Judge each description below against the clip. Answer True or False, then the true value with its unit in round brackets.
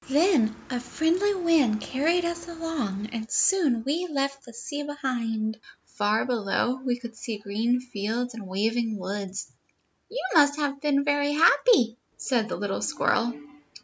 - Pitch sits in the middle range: False (250 Hz)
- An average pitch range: True (4.9 semitones)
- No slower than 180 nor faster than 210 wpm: False (145 wpm)